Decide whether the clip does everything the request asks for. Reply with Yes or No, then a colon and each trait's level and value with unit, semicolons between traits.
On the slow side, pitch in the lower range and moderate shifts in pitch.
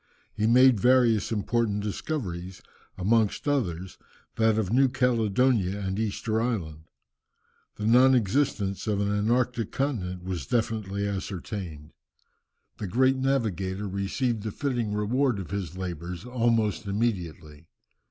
Yes: slow, 120 wpm; low, 105 Hz; average, 4.2 semitones